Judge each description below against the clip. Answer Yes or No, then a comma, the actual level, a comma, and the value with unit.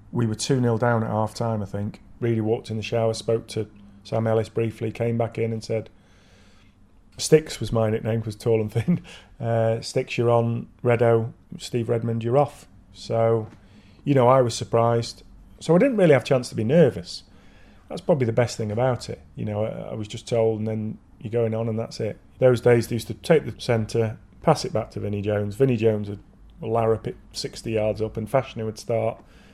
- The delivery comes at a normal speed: No, fast, 210 wpm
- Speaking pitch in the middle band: No, low, 115 Hz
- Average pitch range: No, narrow, 1.6 semitones